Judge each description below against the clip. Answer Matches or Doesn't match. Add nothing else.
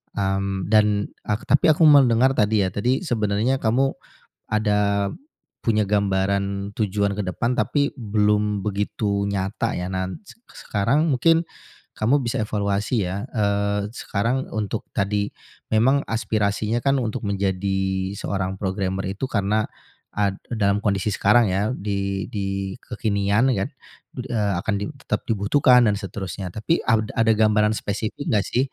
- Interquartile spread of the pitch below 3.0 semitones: Matches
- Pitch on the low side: Matches